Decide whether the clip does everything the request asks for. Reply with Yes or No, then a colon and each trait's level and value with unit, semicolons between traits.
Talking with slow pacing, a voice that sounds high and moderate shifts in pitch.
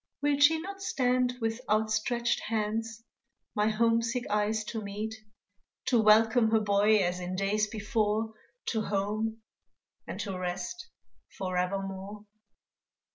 No: slow, 120 wpm; high, 215 Hz; narrow, 2.0 semitones